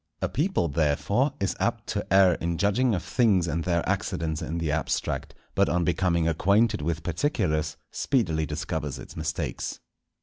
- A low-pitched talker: Yes, very low, 85 Hz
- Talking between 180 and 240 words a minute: No, average, 160 wpm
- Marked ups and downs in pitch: No, average, 4.1 semitones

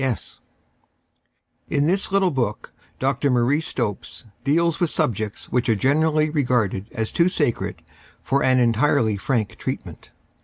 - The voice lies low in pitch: Yes, low, 130 Hz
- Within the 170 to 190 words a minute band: No, average, 140 wpm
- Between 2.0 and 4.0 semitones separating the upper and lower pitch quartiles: No, average, 5.0 semitones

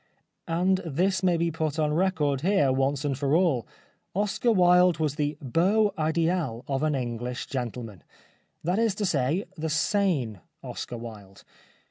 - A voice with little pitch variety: No, wide, 5.4 semitones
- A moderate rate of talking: Yes, average, 150 wpm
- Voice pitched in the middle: Yes, medium, 155 Hz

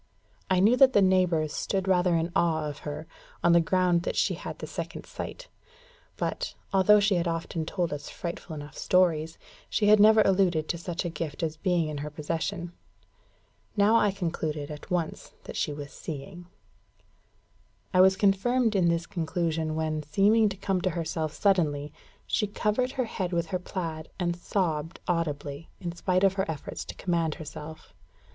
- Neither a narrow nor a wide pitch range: Yes, average, 3.4 semitones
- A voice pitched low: No, medium, 175 Hz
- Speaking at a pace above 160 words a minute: Yes, average, 175 wpm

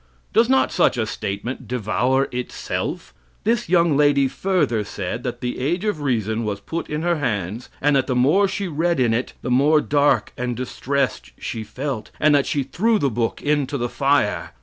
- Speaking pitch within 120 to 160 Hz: Yes, low, 135 Hz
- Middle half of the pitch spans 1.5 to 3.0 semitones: No, average, 4.0 semitones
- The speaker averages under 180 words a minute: No, average, 190 wpm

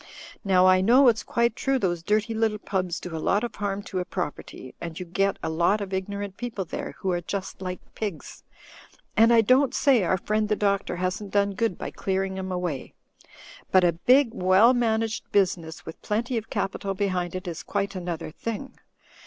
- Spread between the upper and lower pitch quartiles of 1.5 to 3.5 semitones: Yes, average, 3.2 semitones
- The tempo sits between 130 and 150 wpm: No, average, 200 wpm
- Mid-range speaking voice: No, high, 195 Hz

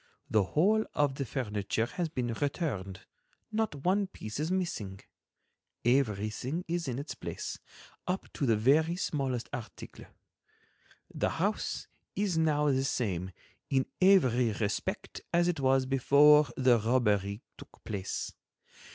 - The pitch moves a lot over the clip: Yes, wide, 6.4 semitones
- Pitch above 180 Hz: No, low, 135 Hz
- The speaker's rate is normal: No, slow, 125 wpm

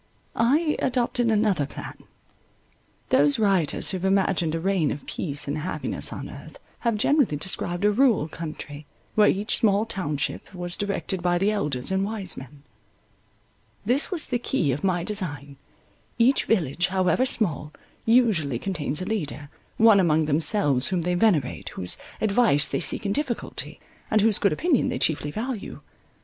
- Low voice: No, high, 190 Hz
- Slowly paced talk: No, average, 160 wpm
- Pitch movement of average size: No, wide, 6.3 semitones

